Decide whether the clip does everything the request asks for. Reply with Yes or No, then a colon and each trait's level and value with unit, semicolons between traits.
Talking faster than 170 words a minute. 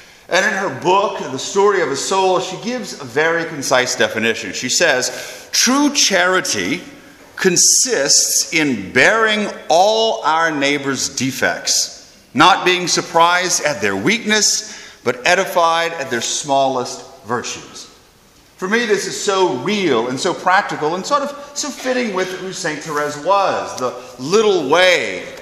No: average, 140 wpm